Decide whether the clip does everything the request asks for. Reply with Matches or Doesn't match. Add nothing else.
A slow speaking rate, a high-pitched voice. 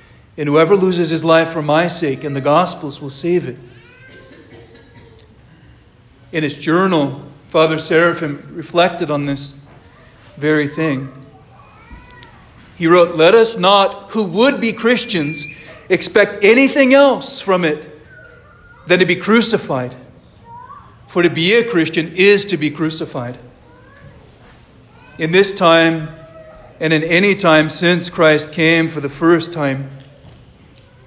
Doesn't match